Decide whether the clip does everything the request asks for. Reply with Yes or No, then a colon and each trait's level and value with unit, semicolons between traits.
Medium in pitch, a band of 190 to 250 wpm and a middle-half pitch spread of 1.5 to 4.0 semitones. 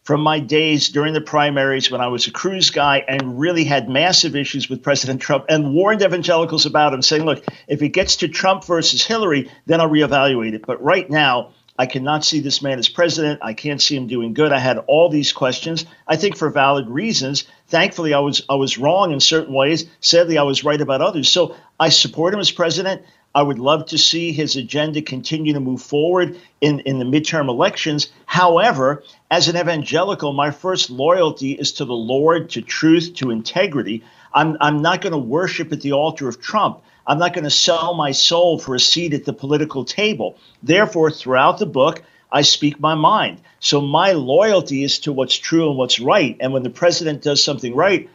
Yes: medium, 150 Hz; fast, 205 wpm; average, 3.2 semitones